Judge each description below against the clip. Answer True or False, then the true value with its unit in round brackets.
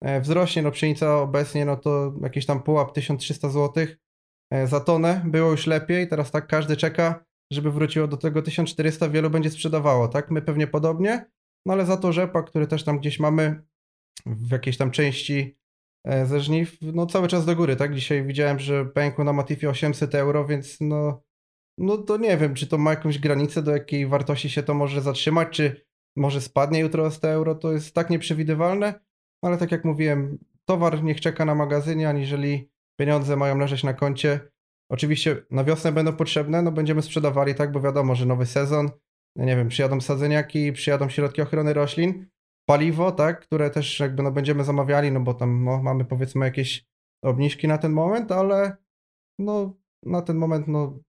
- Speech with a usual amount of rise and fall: False (2.1 semitones)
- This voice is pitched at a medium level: True (150 Hz)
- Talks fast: True (175 wpm)